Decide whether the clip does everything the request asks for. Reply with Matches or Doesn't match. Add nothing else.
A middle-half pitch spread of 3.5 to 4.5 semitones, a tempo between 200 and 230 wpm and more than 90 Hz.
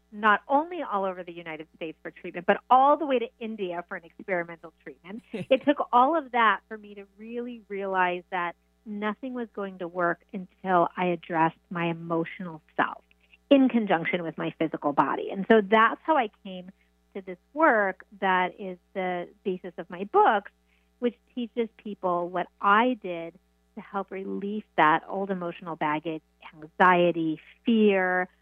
Doesn't match